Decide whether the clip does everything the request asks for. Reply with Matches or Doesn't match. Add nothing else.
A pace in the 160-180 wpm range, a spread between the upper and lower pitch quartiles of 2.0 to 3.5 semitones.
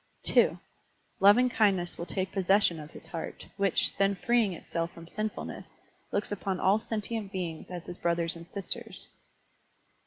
Doesn't match